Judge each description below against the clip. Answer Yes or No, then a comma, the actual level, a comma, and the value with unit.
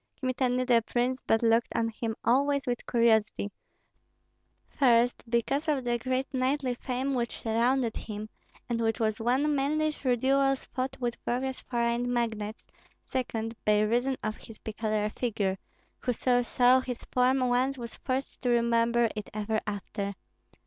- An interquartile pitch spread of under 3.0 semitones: Yes, narrow, 2.4 semitones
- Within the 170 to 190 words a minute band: No, average, 150 wpm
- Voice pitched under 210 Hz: No, high, 240 Hz